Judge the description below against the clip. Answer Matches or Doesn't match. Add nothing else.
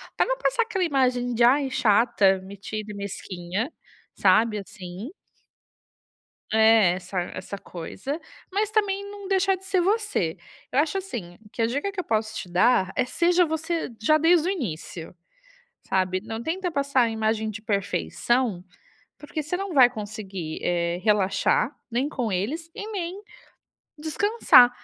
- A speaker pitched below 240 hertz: Doesn't match